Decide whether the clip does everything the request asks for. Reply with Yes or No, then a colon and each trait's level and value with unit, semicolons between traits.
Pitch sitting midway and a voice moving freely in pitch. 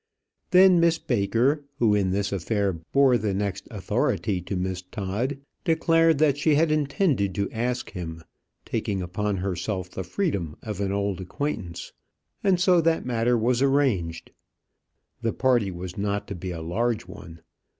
No: low, 105 Hz; wide, 6.9 semitones